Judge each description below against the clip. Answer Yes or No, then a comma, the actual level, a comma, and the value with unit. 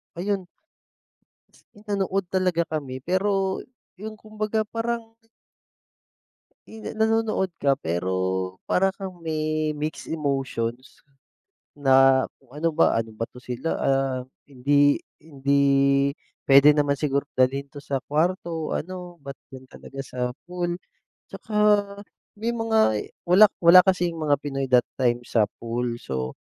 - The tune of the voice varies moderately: No, wide, 5.7 semitones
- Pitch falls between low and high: Yes, medium, 150 Hz